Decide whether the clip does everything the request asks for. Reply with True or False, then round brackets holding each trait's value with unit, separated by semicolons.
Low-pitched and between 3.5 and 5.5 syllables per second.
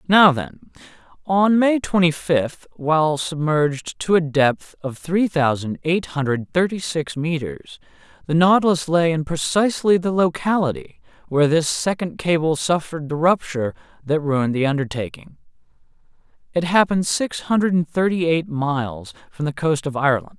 False (160 Hz; 4.8 syllables/s)